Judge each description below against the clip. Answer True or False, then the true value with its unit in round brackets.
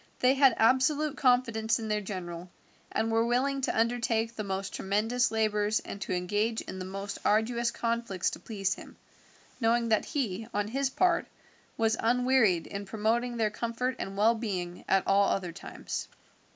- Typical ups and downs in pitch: True (3.2 semitones)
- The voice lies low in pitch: False (225 Hz)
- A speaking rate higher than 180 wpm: False (165 wpm)